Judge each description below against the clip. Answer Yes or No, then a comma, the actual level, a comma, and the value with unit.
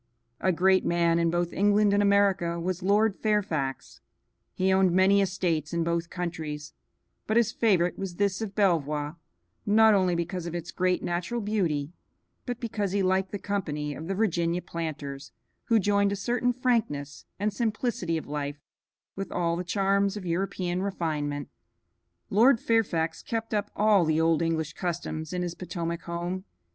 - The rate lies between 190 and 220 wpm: No, average, 160 wpm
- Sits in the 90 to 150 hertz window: No, medium, 180 Hz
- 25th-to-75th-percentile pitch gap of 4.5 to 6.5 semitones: No, average, 3.3 semitones